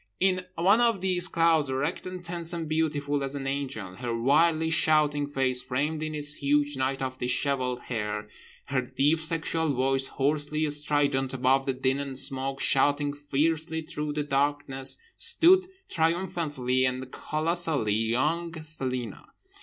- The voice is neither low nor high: Yes, medium, 145 Hz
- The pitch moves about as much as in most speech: Yes, average, 3.4 semitones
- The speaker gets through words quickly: No, average, 140 wpm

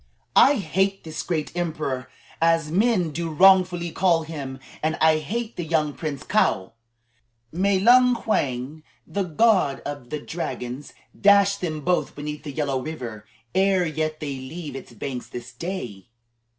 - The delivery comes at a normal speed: Yes, average, 150 wpm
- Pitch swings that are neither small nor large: Yes, average, 4.7 semitones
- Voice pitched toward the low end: No, medium, 160 Hz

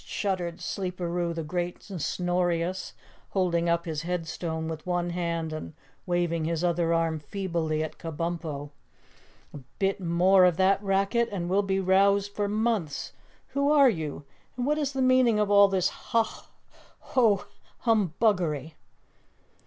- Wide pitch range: No, average, 3.2 semitones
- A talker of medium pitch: Yes, medium, 180 Hz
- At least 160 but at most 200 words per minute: No, average, 145 wpm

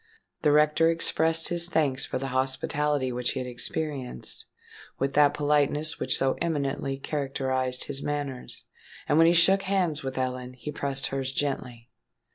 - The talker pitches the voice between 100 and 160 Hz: Yes, medium, 140 Hz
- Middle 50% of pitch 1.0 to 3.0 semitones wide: Yes, narrow, 2.6 semitones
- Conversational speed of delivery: Yes, average, 155 wpm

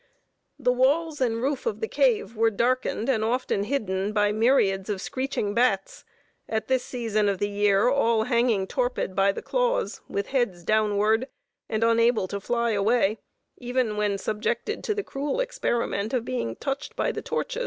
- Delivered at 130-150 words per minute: No, average, 170 wpm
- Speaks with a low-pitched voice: No, high, 230 Hz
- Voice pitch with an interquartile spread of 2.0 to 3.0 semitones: No, average, 4.0 semitones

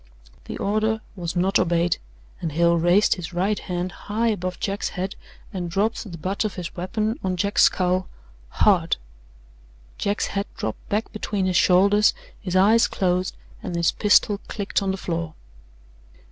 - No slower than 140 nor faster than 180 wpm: Yes, average, 160 wpm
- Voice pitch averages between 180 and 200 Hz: Yes, medium, 185 Hz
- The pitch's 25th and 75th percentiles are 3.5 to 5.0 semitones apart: No, average, 2.7 semitones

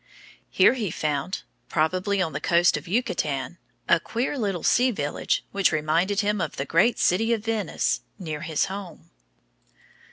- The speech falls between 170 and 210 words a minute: No, average, 155 wpm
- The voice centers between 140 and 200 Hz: Yes, medium, 185 Hz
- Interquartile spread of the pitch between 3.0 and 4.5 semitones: No, average, 4.9 semitones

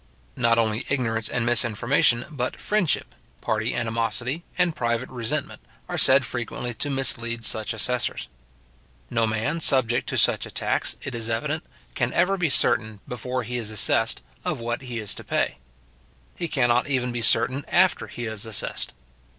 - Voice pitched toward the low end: Yes, low, 120 Hz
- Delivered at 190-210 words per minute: No, average, 160 wpm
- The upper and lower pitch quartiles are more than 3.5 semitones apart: No, average, 2.8 semitones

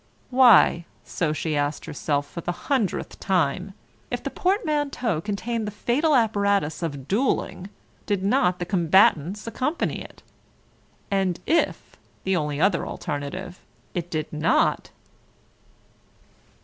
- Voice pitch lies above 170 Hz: Yes, high, 190 Hz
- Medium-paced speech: No, slow, 120 wpm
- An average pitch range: No, wide, 6.2 semitones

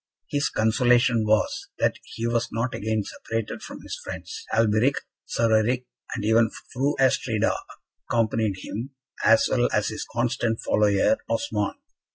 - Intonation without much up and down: Yes, narrow, 2.1 semitones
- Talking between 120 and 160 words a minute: Yes, average, 140 wpm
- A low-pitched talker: Yes, low, 115 Hz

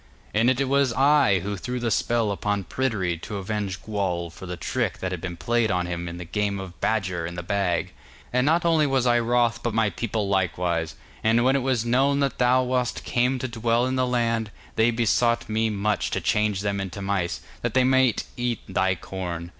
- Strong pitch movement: No, average, 4.6 semitones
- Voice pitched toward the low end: Yes, low, 110 Hz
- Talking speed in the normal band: No, fast, 210 wpm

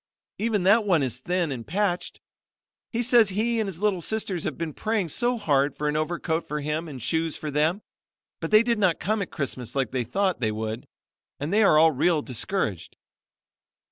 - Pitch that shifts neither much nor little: No, wide, 6.1 semitones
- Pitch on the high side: No, medium, 165 Hz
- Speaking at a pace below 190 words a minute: No, average, 195 wpm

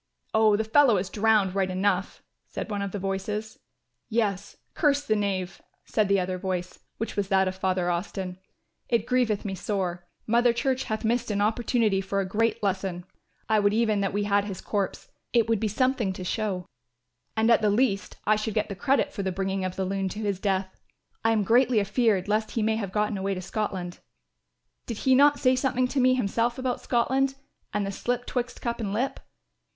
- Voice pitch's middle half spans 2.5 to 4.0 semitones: Yes, average, 3.3 semitones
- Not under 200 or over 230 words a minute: Yes, fast, 205 wpm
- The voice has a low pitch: No, high, 210 Hz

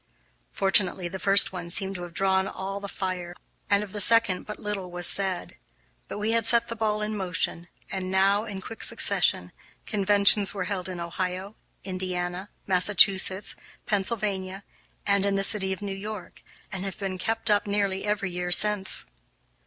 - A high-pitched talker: Yes, high, 195 Hz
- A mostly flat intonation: Yes, narrow, 1.9 semitones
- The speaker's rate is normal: Yes, average, 170 wpm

